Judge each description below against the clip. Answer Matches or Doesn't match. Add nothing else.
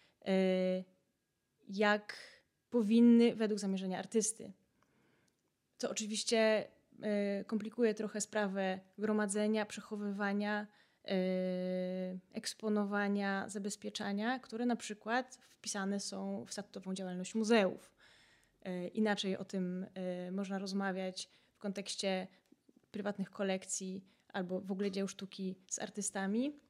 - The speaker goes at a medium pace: Doesn't match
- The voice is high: Matches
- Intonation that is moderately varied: Doesn't match